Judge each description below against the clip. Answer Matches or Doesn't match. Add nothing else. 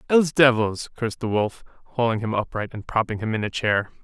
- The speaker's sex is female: Doesn't match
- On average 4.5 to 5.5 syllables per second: Doesn't match